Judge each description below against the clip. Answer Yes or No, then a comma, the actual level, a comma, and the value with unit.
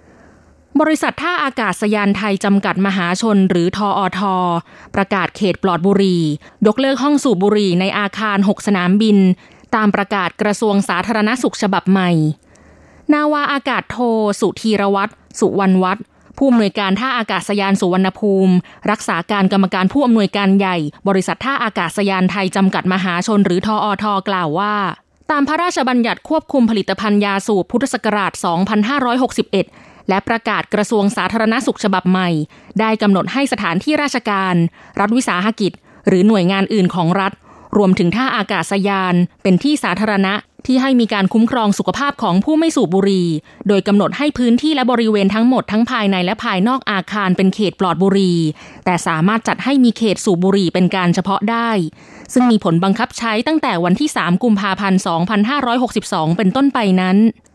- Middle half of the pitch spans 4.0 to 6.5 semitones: No, average, 3.3 semitones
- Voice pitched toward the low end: No, high, 200 Hz